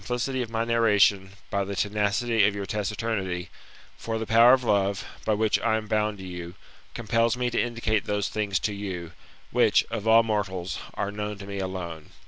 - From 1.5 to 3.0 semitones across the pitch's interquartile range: Yes, narrow, 2.6 semitones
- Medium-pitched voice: No, low, 105 Hz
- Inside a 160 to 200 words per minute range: Yes, average, 195 wpm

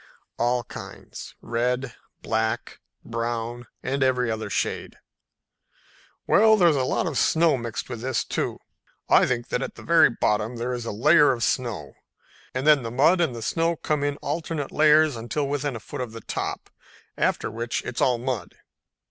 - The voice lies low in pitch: Yes, low, 125 Hz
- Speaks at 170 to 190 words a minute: Yes, average, 175 wpm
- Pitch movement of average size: Yes, average, 3.9 semitones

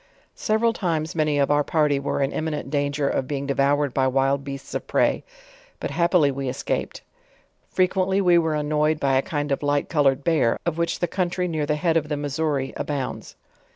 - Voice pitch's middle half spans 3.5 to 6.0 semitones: No, average, 2.8 semitones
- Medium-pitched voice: Yes, medium, 150 Hz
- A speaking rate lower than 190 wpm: No, average, 200 wpm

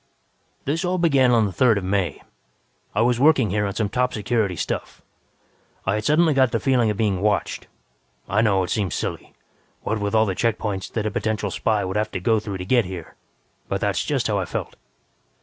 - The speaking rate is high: Yes, fast, 215 wpm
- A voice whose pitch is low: Yes, low, 110 Hz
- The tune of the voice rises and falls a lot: No, average, 3.7 semitones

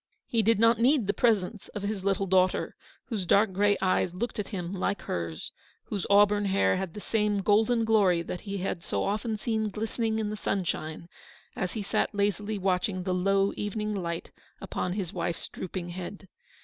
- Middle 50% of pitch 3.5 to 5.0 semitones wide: No, narrow, 2.5 semitones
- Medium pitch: No, high, 200 Hz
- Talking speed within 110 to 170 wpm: No, average, 185 wpm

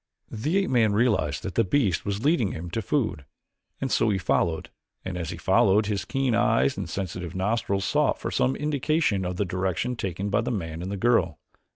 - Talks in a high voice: No, low, 100 Hz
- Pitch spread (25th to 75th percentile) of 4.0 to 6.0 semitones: Yes, average, 5.0 semitones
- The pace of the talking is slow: No, fast, 205 wpm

